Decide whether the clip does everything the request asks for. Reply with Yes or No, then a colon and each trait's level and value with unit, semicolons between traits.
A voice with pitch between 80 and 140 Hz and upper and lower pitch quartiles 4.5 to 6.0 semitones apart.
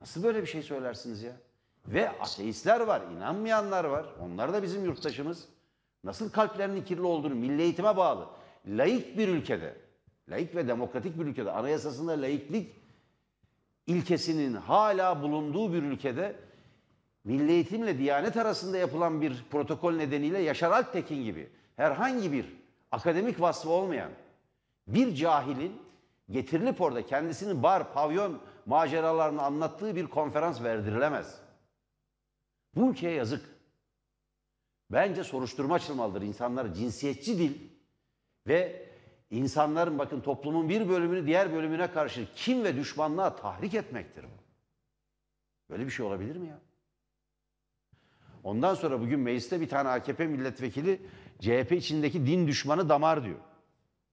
No: medium, 155 Hz; average, 4.8 semitones